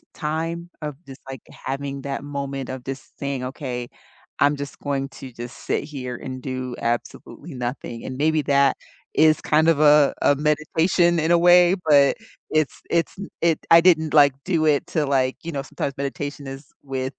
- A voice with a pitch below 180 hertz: Yes, medium, 140 Hz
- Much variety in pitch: No, average, 2.8 semitones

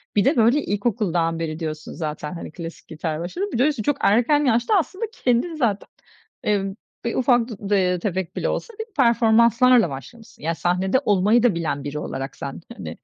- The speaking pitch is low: No, high, 210 Hz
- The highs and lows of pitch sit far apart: Yes, wide, 6.6 semitones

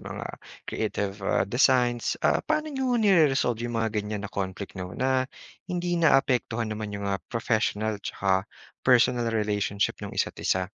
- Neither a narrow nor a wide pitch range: Yes, average, 4.3 semitones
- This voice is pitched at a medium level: No, low, 115 Hz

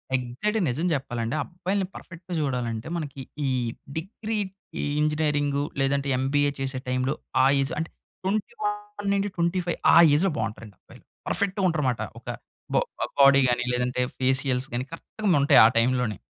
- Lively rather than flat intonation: Yes, wide, 6.1 semitones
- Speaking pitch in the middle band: Yes, medium, 145 Hz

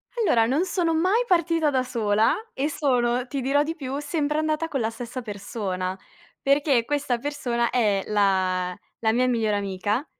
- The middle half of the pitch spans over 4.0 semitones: Yes, average, 5.3 semitones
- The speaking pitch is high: Yes, very high, 250 Hz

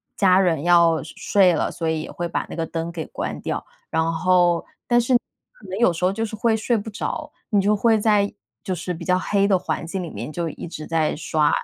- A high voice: No, medium, 180 Hz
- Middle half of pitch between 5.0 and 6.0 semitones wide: No, average, 3.7 semitones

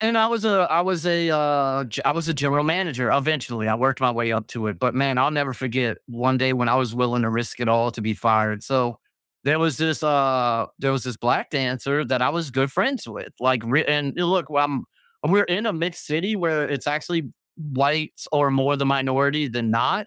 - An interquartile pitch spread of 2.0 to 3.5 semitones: No, average, 4.1 semitones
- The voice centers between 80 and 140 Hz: Yes, low, 135 Hz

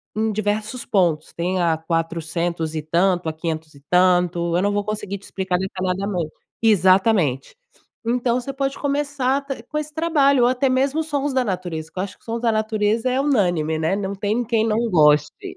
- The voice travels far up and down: Yes, wide, 6.1 semitones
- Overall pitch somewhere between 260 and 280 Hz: No, high, 200 Hz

